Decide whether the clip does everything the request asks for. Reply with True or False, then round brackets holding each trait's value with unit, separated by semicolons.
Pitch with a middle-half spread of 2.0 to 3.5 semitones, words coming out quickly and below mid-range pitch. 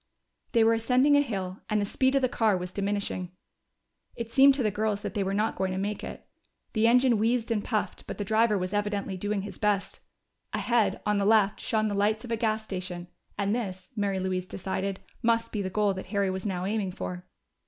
False (2.8 semitones; 220 wpm; 205 Hz)